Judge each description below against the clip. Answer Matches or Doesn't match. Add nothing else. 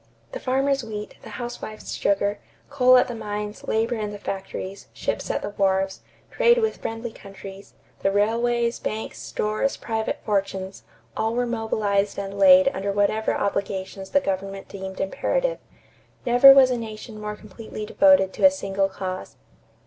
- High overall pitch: Matches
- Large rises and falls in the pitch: Doesn't match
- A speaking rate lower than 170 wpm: Matches